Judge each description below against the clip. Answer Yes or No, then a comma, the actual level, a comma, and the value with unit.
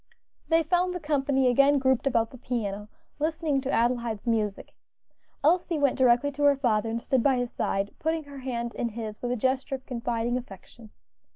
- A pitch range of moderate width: Yes, average, 3.5 semitones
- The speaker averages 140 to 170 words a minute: No, average, 185 wpm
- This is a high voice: Yes, very high, 255 Hz